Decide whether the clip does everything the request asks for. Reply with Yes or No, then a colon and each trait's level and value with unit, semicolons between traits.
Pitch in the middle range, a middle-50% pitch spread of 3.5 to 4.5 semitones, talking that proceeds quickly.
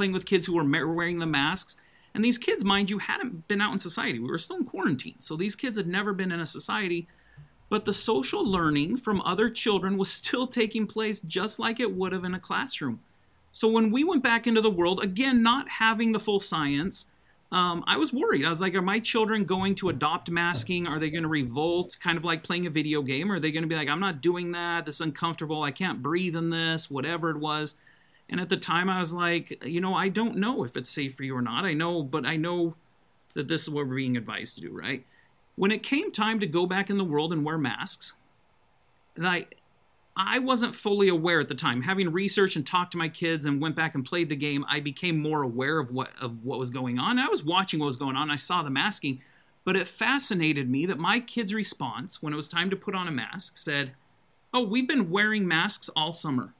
No: medium, 175 Hz; average, 5.0 semitones; fast, 245 wpm